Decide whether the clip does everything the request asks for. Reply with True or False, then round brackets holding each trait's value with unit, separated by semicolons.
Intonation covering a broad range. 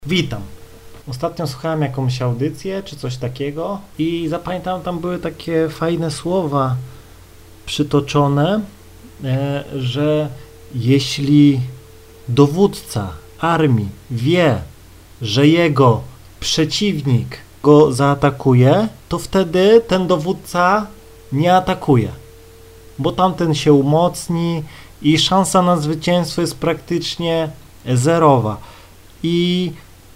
True (6.0 semitones)